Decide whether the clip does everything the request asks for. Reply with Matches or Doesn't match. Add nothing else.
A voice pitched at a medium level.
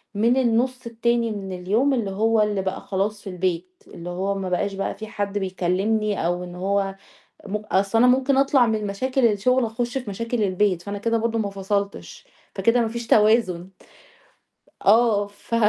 Doesn't match